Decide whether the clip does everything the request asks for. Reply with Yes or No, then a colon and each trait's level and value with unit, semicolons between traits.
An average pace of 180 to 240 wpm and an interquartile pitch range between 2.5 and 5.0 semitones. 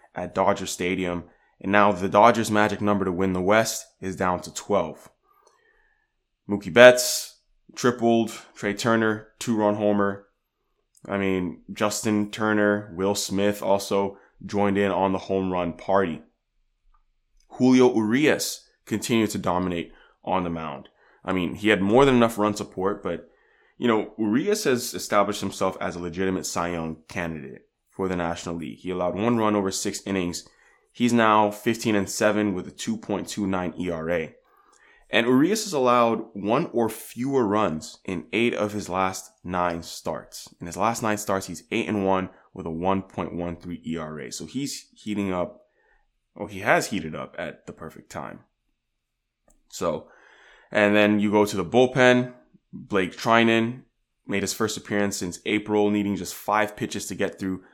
No: average, 160 wpm; average, 3.0 semitones